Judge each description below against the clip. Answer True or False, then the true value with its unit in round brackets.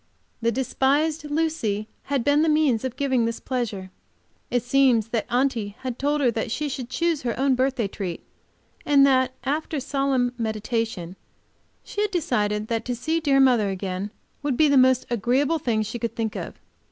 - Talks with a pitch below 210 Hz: False (255 Hz)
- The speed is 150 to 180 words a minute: True (175 wpm)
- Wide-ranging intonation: False (3.9 semitones)